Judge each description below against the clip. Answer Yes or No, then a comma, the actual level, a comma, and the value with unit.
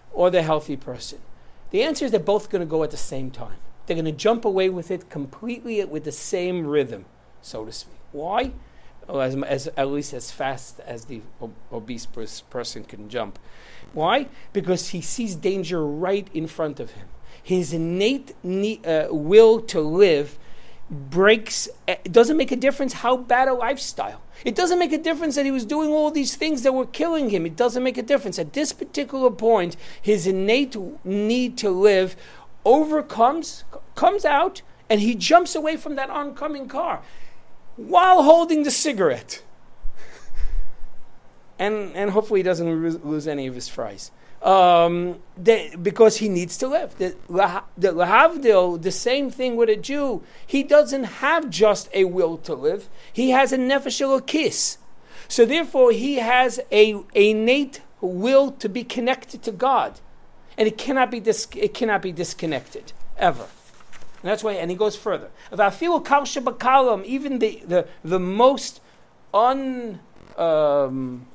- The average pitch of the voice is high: Yes, high, 215 Hz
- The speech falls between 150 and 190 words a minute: Yes, average, 165 wpm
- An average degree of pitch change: No, wide, 7.3 semitones